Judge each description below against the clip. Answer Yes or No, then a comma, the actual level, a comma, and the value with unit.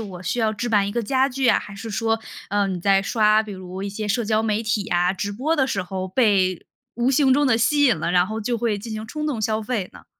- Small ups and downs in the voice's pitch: No, average, 3.3 semitones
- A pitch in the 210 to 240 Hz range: Yes, high, 215 Hz